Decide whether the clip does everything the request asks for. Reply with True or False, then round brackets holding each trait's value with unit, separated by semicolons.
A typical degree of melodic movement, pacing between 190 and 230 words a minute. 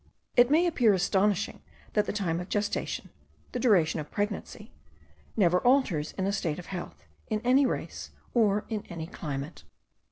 False (4.4 semitones; 160 wpm)